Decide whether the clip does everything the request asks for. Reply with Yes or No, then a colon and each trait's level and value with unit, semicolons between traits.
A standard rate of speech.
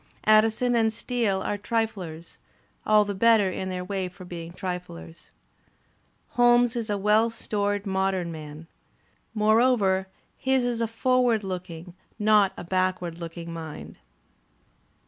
No: slow, 130 wpm